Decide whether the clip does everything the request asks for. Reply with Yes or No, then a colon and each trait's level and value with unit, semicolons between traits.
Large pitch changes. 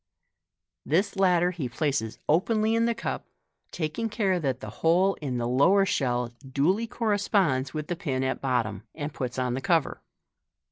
Yes: wide, 6.8 semitones